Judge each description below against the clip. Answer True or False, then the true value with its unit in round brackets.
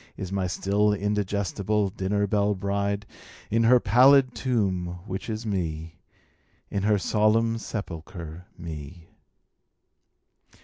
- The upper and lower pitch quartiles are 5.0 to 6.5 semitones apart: False (2.7 semitones)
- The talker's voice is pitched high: False (100 Hz)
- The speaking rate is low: True (105 wpm)